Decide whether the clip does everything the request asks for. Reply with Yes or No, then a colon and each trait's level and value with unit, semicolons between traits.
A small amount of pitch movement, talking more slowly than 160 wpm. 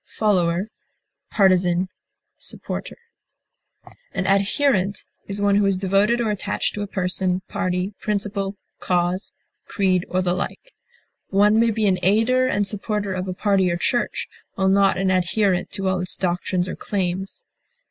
Yes: narrow, 2.0 semitones; average, 145 wpm